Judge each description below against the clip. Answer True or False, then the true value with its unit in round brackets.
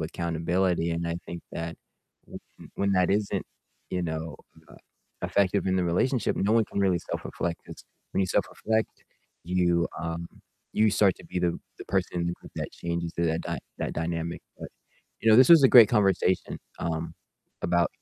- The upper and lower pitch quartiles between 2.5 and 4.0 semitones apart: True (2.8 semitones)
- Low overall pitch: True (85 Hz)